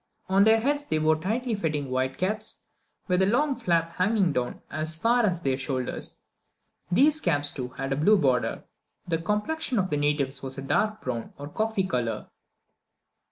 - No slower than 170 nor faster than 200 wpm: Yes, average, 175 wpm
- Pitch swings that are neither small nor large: No, wide, 7.4 semitones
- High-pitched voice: No, medium, 170 Hz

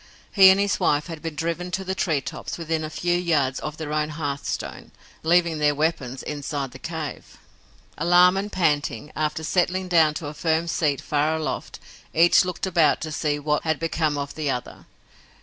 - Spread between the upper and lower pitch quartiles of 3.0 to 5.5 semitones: No, narrow, 2.6 semitones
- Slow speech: No, average, 185 wpm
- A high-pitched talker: No, medium, 160 Hz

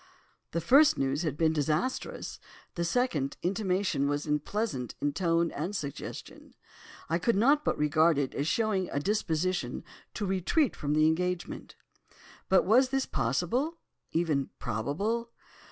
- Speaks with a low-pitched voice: No, medium, 170 Hz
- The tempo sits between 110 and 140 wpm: Yes, slow, 135 wpm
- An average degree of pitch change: No, wide, 6.1 semitones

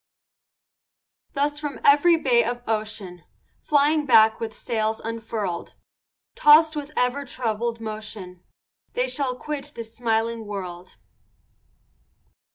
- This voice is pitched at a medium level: No, high, 230 Hz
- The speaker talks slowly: Yes, slow, 105 wpm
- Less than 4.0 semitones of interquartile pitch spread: No, average, 4.7 semitones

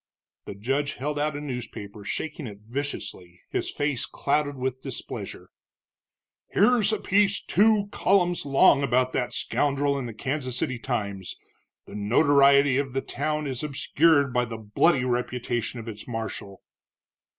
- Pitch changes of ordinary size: Yes, average, 3.5 semitones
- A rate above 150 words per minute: No, average, 145 wpm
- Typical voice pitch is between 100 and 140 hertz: Yes, low, 135 Hz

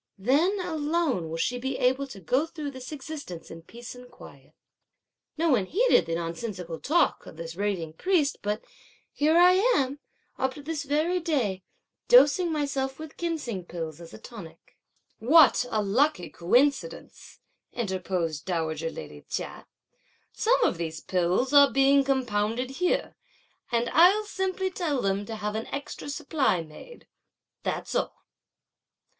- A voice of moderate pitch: No, very high, 260 Hz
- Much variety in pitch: Yes, wide, 8.5 semitones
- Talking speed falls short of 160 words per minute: Yes, average, 150 wpm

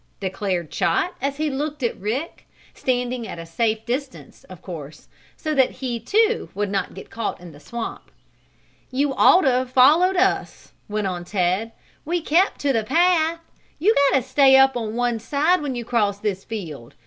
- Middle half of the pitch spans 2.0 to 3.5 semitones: No, wide, 5.6 semitones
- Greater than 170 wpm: Yes, average, 185 wpm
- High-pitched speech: Yes, very high, 250 Hz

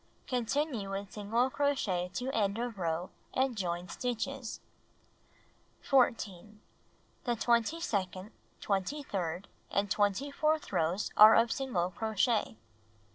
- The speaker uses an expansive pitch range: No, average, 4.8 semitones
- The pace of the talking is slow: Yes, slow, 115 wpm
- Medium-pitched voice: No, high, 215 Hz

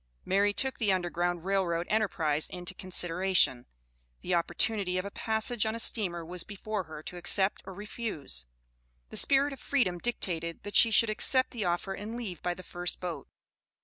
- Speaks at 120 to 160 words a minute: No, average, 180 wpm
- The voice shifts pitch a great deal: No, average, 3.7 semitones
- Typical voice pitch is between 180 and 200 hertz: Yes, high, 190 Hz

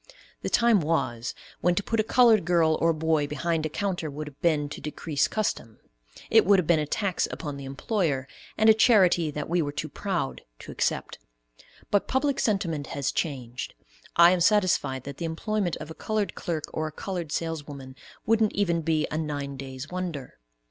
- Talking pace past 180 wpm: Yes, average, 190 wpm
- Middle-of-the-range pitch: Yes, medium, 165 Hz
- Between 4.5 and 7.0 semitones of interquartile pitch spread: Yes, average, 4.8 semitones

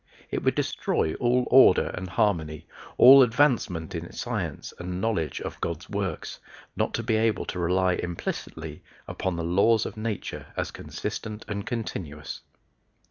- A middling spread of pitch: Yes, average, 4.8 semitones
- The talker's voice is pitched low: Yes, very low, 95 Hz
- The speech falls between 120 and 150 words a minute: Yes, average, 145 wpm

